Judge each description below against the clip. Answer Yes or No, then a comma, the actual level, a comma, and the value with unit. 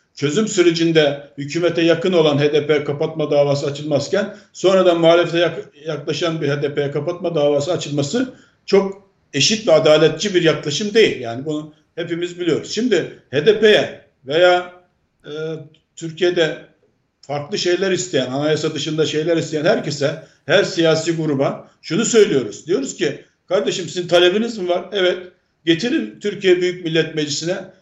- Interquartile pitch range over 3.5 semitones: No, average, 3.0 semitones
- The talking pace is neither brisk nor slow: Yes, average, 125 wpm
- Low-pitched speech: No, medium, 165 Hz